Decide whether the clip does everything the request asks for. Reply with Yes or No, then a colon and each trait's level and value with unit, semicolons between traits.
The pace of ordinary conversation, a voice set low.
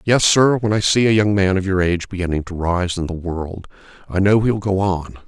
No: fast, 250 wpm; very low, 95 Hz